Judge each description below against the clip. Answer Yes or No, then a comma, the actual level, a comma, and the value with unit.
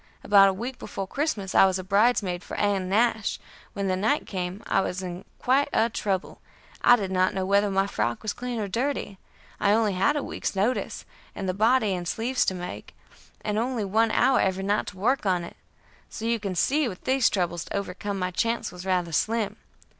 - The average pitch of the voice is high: Yes, high, 200 Hz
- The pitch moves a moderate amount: Yes, average, 3.4 semitones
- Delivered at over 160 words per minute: Yes, fast, 205 wpm